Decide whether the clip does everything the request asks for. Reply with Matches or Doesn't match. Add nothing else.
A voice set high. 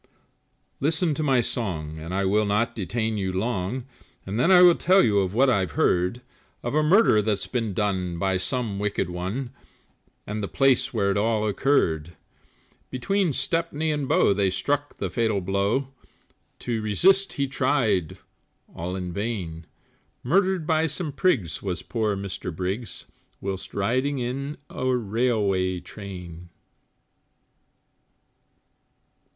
Doesn't match